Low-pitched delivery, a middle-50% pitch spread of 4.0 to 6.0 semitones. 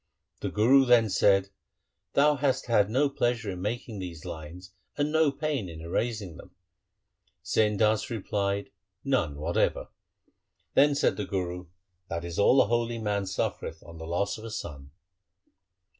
Yes: low, 105 Hz; average, 5.2 semitones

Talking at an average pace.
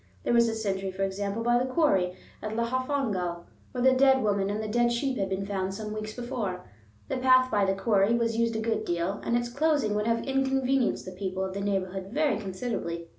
No: fast, 220 wpm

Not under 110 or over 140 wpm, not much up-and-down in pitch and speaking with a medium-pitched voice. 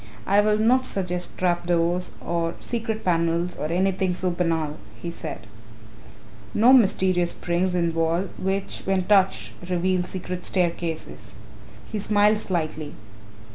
Yes: slow, 135 wpm; narrow, 2.3 semitones; medium, 180 Hz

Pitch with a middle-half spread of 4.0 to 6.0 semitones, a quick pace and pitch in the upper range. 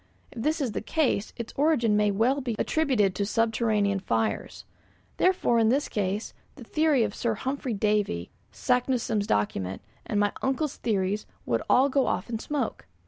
No: average, 4.5 semitones; average, 165 wpm; high, 225 Hz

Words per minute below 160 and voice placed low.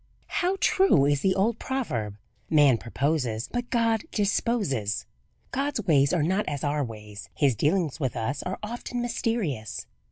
No: average, 150 wpm; medium, 155 Hz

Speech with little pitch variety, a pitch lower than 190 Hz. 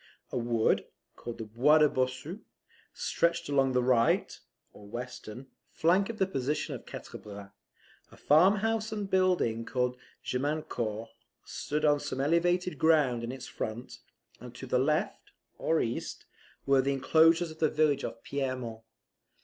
No: average, 4.9 semitones; low, 135 Hz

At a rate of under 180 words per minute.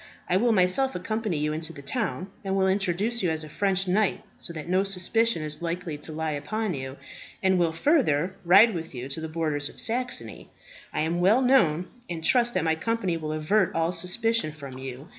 No: fast, 205 wpm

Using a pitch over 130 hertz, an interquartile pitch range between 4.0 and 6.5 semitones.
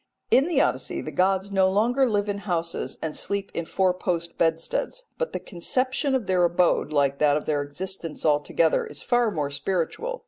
Yes: medium, 185 Hz; average, 4.5 semitones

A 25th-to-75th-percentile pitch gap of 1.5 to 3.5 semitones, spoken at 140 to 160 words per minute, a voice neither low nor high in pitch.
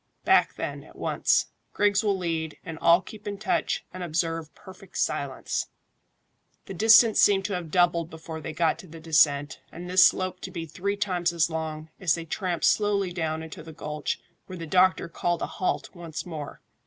No: average, 2.8 semitones; average, 190 wpm; medium, 175 Hz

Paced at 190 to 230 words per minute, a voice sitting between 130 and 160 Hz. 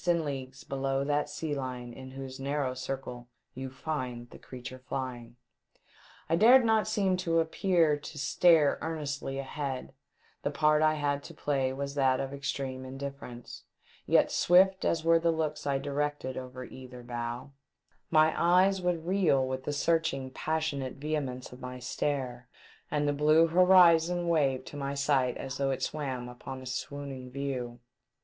No: average, 160 wpm; medium, 140 Hz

